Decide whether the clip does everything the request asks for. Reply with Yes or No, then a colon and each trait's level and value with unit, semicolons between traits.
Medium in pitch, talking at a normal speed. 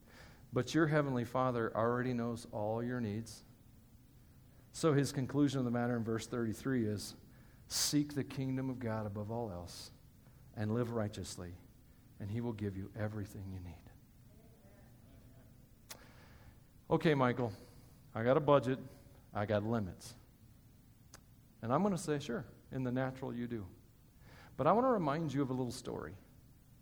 No: low, 120 Hz; average, 150 wpm